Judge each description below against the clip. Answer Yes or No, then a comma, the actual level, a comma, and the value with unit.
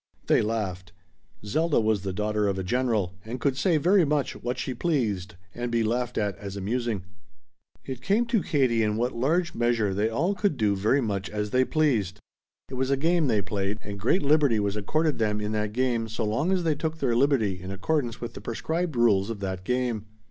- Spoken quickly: Yes, fast, 210 wpm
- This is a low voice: Yes, low, 115 Hz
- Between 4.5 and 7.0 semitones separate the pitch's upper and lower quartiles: Yes, average, 5.3 semitones